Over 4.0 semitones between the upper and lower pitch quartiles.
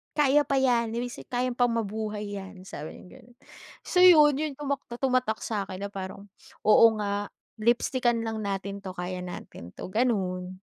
Yes: average, 4.5 semitones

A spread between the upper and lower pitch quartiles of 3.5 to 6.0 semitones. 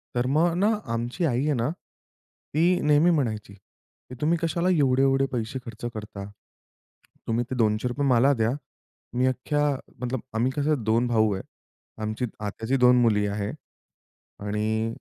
Yes: average, 4.5 semitones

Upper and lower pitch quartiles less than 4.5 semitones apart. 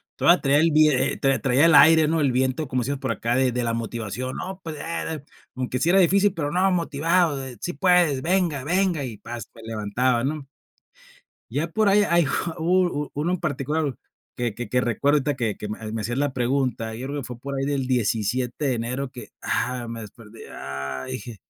No: average, 5.0 semitones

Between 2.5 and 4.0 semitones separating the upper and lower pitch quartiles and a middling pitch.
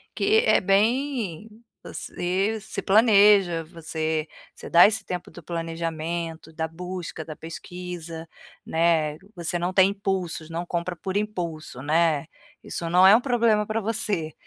Yes: average, 3.7 semitones; medium, 175 Hz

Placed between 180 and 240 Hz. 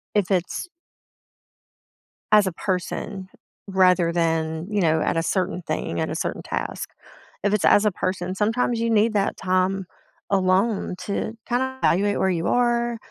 Yes: high, 190 Hz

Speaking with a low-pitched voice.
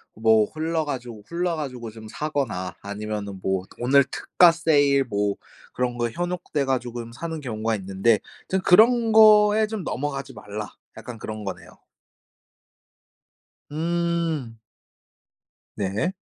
Yes: low, 130 Hz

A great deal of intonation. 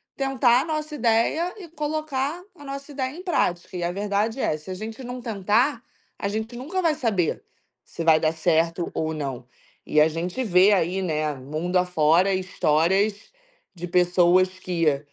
Yes: wide, 7.4 semitones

